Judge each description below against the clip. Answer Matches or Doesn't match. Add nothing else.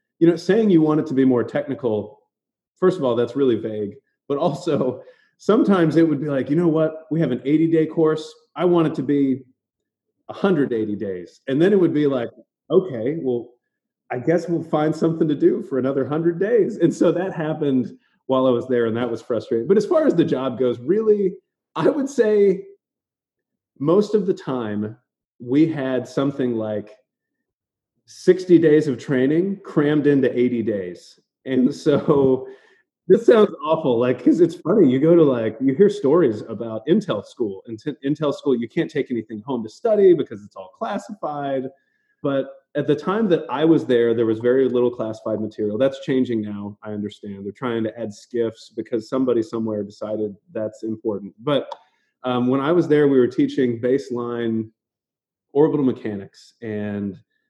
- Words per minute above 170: Matches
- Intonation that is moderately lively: Doesn't match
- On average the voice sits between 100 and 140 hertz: Matches